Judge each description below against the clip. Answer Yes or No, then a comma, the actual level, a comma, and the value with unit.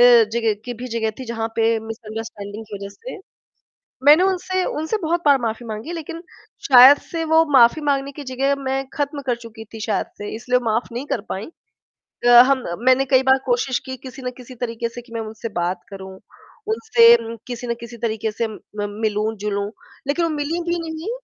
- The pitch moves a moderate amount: Yes, average, 4.5 semitones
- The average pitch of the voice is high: Yes, high, 245 Hz